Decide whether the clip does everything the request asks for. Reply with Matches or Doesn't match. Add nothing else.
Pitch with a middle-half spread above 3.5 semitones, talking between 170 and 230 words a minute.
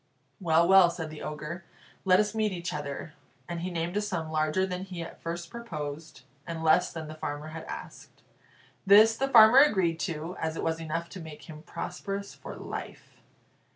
Doesn't match